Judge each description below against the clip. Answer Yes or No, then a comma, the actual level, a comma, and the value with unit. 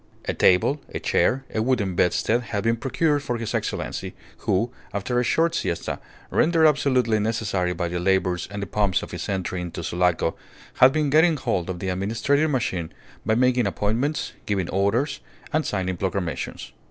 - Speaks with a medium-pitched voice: No, low, 110 Hz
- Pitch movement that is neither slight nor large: No, wide, 6.0 semitones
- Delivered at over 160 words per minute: Yes, average, 170 wpm